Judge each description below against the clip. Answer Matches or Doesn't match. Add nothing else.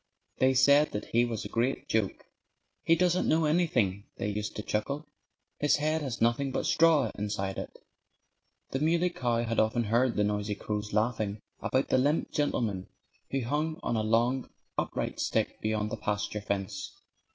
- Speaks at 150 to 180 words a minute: Matches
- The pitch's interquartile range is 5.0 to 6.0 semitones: Matches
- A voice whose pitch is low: Matches